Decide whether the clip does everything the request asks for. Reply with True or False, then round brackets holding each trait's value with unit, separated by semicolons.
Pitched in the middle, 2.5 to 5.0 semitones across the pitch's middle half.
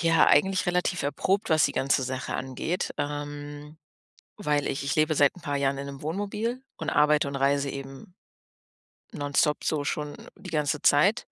True (145 Hz; 2.9 semitones)